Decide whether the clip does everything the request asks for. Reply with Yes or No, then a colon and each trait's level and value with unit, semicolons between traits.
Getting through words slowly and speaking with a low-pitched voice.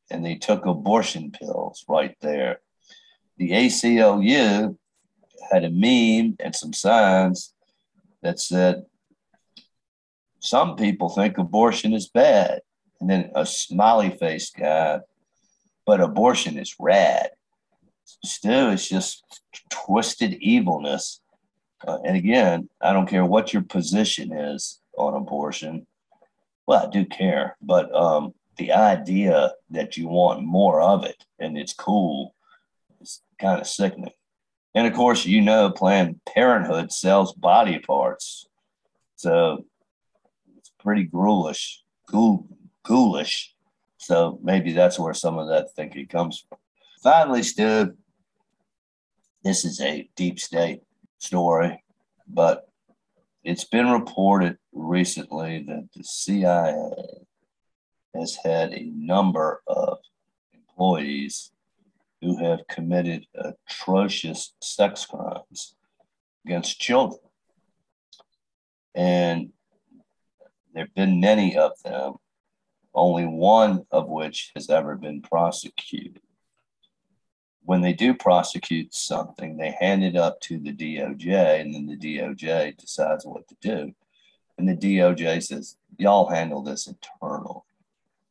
Yes: slow, 115 wpm; very low, 95 Hz